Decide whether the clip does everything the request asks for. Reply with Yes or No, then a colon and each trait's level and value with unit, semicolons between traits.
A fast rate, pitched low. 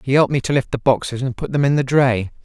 Yes: fast, 320 wpm; low, 130 Hz